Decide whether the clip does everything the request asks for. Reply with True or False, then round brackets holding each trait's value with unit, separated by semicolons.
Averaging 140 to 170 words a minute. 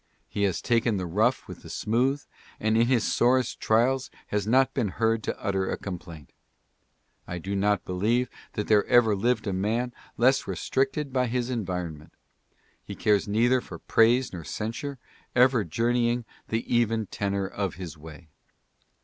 True (165 wpm)